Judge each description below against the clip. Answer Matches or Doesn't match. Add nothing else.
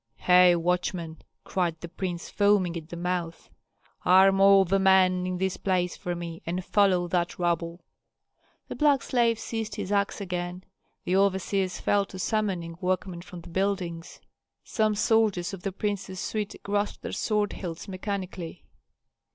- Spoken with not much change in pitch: Matches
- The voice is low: Doesn't match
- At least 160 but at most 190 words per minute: Doesn't match